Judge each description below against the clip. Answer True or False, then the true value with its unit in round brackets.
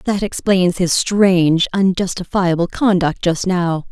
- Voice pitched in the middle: True (180 Hz)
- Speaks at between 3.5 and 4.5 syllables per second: True (4.0 syllables/s)